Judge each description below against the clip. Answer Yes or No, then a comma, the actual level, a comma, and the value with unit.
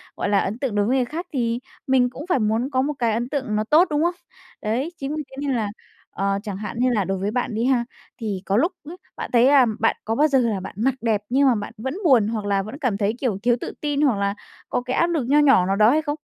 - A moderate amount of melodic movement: Yes, average, 4.7 semitones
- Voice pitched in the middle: No, high, 240 Hz